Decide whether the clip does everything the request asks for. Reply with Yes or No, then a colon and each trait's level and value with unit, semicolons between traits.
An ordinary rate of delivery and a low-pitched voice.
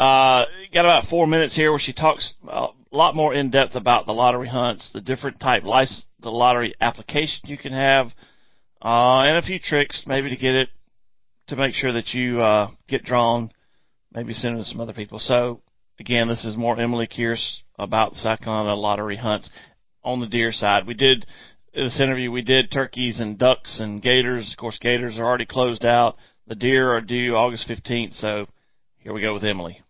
Yes: average, 195 wpm; low, 120 Hz